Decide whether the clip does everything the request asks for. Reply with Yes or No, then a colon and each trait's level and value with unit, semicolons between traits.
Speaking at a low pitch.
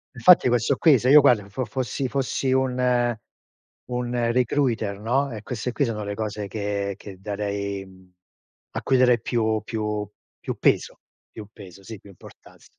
Yes: low, 115 Hz